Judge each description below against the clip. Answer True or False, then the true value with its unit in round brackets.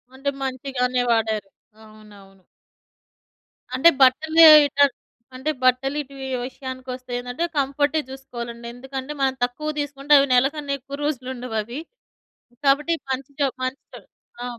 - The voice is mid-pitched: False (265 Hz)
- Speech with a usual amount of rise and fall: False (2.2 semitones)